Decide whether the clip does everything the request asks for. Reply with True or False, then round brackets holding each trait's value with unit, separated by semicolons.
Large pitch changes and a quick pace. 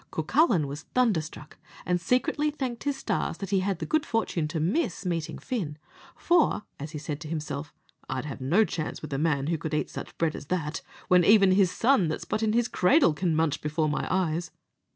True (6.1 semitones; 210 wpm)